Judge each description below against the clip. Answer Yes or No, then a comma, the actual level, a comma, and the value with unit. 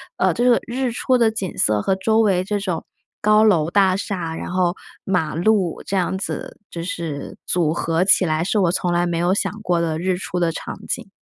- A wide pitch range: No, average, 3.3 semitones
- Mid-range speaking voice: Yes, medium, 180 Hz